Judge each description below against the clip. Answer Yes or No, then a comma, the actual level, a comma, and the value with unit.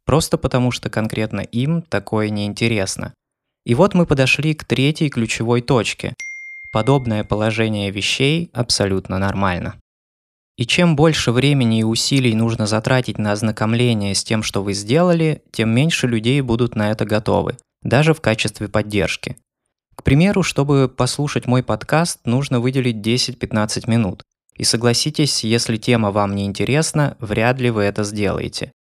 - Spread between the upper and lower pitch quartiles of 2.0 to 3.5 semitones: No, average, 4.3 semitones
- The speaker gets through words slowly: No, average, 140 wpm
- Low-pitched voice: Yes, low, 120 Hz